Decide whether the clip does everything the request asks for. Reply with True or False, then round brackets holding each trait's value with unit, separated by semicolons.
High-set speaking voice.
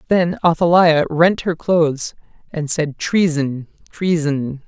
False (160 Hz)